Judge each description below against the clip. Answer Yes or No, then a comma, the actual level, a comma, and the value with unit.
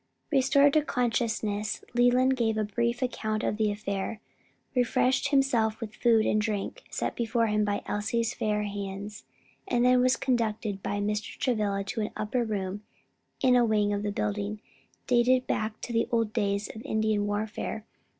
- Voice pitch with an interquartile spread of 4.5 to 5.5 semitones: No, narrow, 2.6 semitones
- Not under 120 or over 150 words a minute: No, average, 165 wpm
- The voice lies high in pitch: Yes, high, 220 Hz